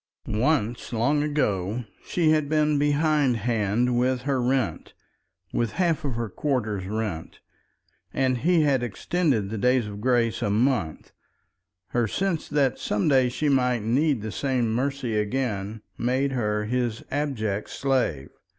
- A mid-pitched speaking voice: No, low, 125 Hz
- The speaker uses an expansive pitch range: No, average, 4.4 semitones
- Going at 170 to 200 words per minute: No, average, 140 wpm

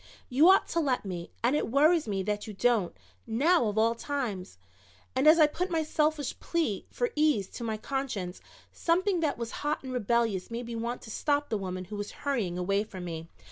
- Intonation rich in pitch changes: Yes, wide, 6.6 semitones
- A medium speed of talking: No, fast, 210 wpm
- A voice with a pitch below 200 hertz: No, high, 235 Hz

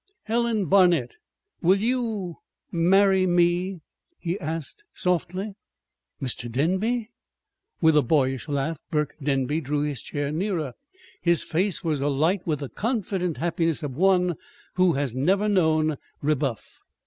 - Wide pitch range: No, average, 4.5 semitones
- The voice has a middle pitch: Yes, medium, 170 Hz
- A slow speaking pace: Yes, slow, 125 wpm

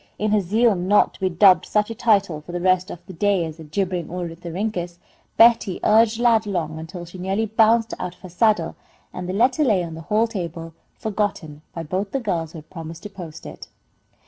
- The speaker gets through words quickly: Yes, fast, 215 wpm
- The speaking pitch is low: No, medium, 185 Hz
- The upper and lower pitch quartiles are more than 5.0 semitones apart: No, average, 4.0 semitones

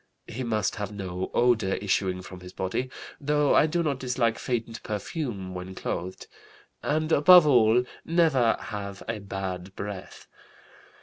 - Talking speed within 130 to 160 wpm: Yes, average, 140 wpm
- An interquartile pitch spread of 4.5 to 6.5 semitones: Yes, wide, 5.6 semitones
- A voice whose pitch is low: Yes, low, 110 Hz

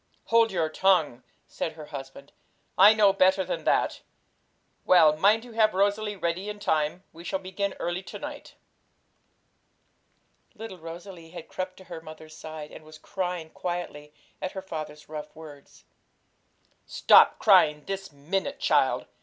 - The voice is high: No, medium, 175 Hz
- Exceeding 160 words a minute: No, average, 145 wpm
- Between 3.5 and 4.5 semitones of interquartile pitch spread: Yes, average, 3.9 semitones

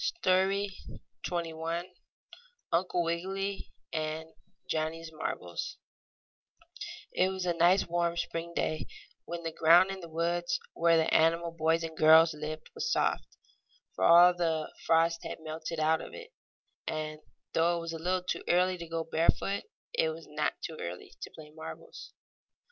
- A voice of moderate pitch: Yes, medium, 165 Hz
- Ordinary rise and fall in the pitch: No, narrow, 1.6 semitones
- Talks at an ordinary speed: Yes, average, 150 wpm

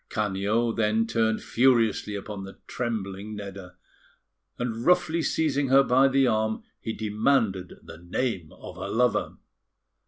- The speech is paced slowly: Yes, slow, 130 wpm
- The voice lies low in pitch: Yes, low, 110 Hz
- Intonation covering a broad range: No, average, 3.7 semitones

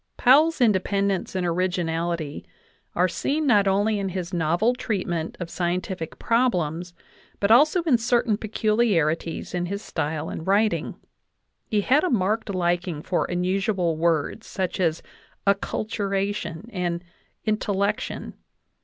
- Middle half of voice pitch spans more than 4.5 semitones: No, average, 3.9 semitones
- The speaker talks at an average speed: No, slow, 120 wpm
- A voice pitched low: No, high, 190 Hz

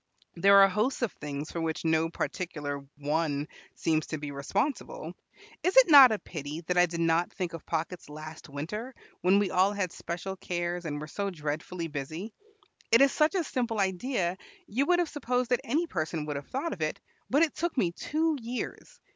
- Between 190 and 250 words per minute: Yes, average, 195 wpm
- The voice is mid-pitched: Yes, medium, 180 Hz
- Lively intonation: Yes, wide, 7.6 semitones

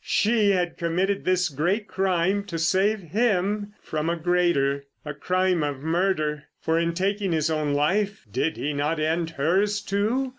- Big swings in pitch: No, average, 4.3 semitones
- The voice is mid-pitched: Yes, medium, 175 Hz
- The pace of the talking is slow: No, average, 160 wpm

